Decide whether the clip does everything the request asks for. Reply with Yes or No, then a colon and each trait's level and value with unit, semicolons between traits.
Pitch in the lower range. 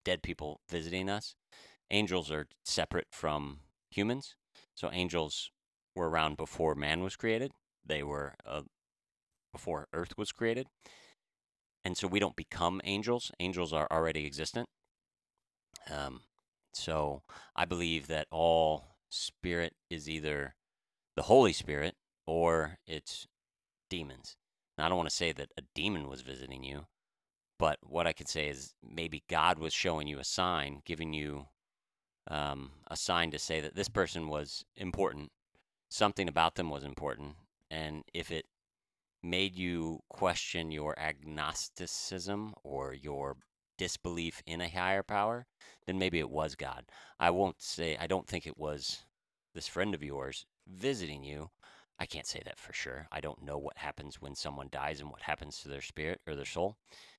Yes: very low, 80 Hz